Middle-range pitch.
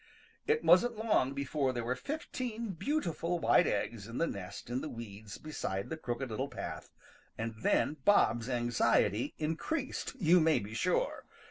Yes: medium, 145 Hz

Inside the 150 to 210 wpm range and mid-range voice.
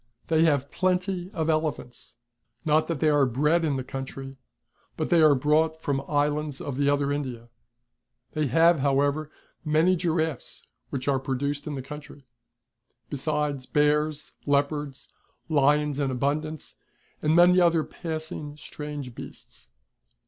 No: average, 140 wpm; medium, 150 Hz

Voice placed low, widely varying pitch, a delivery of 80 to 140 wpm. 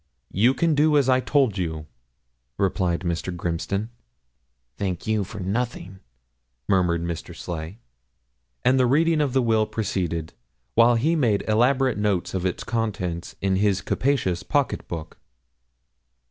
Yes: low, 105 Hz; wide, 6.1 semitones; slow, 135 wpm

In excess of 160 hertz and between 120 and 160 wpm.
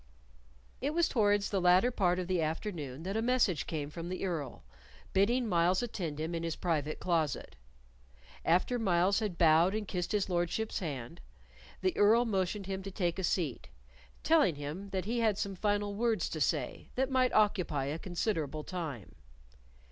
No: medium, 185 Hz; average, 170 wpm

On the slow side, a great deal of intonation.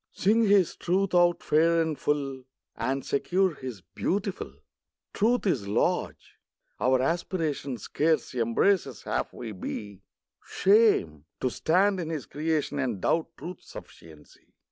Yes: slow, 125 wpm; wide, 6.4 semitones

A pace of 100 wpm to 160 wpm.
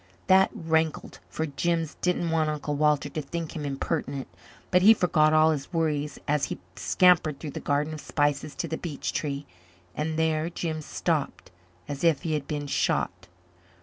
No: average, 175 wpm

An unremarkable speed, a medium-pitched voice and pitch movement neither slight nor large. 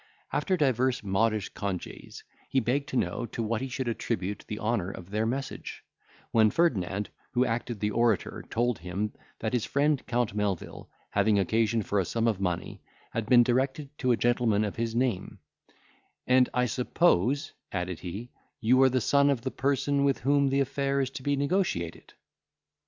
No: average, 175 wpm; low, 120 Hz; average, 4.2 semitones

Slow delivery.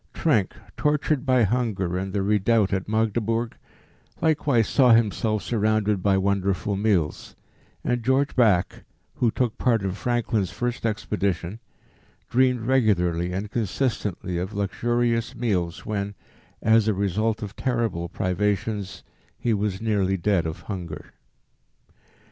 Yes: slow, 125 wpm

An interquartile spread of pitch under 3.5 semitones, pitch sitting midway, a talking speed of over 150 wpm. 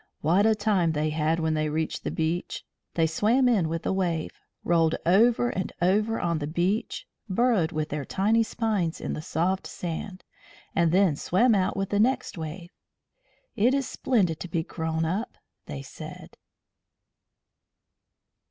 No: average, 4.7 semitones; medium, 180 Hz; average, 160 wpm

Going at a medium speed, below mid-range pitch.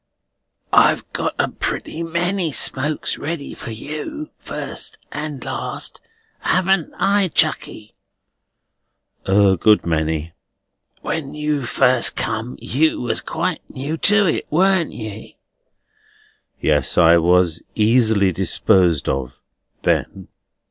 No: slow, 105 wpm; low, 130 Hz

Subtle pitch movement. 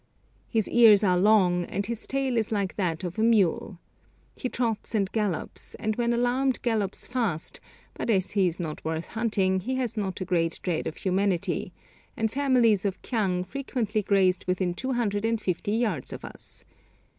No: average, 4.0 semitones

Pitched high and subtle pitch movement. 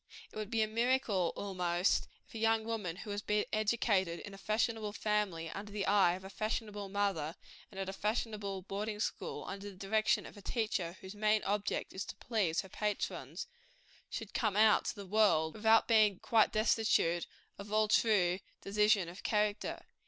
Yes: high, 210 Hz; narrow, 2.1 semitones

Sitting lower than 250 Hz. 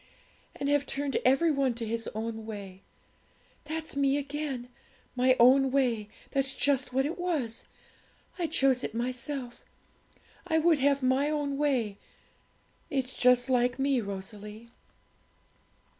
No: very high, 265 Hz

